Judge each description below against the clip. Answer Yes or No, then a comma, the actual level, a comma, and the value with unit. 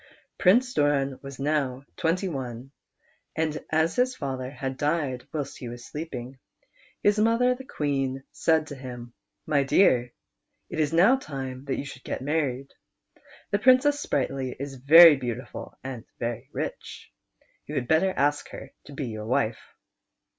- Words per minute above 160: No, average, 155 wpm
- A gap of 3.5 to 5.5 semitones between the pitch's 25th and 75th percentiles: Yes, average, 3.9 semitones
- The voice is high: No, medium, 140 Hz